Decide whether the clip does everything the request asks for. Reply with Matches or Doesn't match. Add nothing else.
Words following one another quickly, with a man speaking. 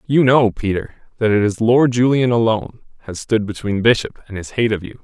Matches